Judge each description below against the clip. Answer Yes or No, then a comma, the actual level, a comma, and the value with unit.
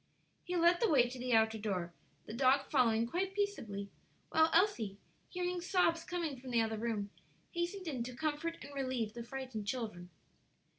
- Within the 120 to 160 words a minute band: No, average, 170 wpm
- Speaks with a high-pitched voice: Yes, very high, 260 Hz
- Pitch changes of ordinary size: No, wide, 7.2 semitones